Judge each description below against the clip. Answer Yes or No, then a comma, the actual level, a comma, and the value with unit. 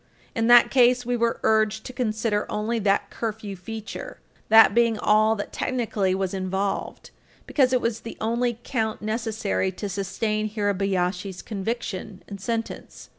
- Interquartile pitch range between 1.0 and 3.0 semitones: Yes, average, 2.7 semitones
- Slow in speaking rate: No, average, 145 wpm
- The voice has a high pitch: Yes, high, 215 Hz